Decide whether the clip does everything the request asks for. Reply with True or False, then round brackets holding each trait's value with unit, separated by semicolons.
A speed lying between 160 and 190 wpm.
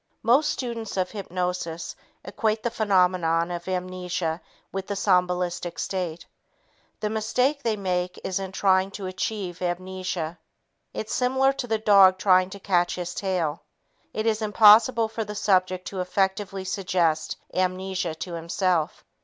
False (140 wpm)